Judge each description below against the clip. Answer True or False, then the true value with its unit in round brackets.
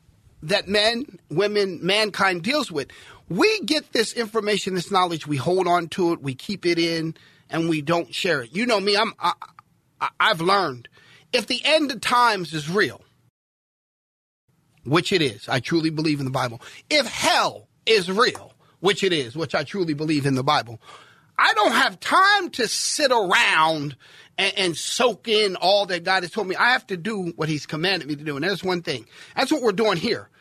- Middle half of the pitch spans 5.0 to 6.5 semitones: True (5.6 semitones)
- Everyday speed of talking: True (195 wpm)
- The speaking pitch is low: False (185 Hz)